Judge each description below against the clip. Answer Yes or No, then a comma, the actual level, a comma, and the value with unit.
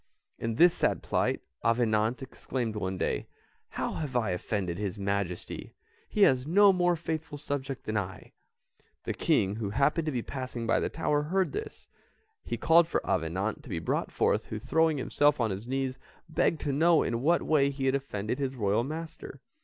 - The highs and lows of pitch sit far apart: Yes, wide, 6.3 semitones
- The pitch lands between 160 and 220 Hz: No, low, 130 Hz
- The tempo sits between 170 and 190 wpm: Yes, average, 185 wpm